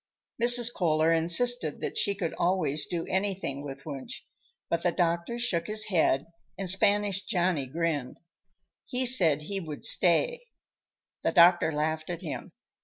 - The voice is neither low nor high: Yes, medium, 175 Hz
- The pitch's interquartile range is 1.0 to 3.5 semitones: No, average, 4.2 semitones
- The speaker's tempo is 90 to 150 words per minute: Yes, average, 145 wpm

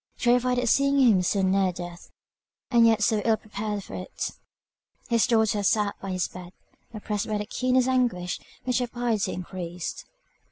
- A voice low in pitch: No, high, 215 Hz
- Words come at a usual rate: Yes, average, 165 wpm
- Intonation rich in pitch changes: No, average, 4.3 semitones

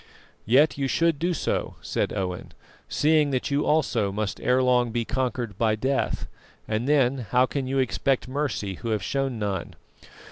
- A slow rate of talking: No, average, 170 wpm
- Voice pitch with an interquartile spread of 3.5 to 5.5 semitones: Yes, average, 4.0 semitones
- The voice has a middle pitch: No, low, 130 Hz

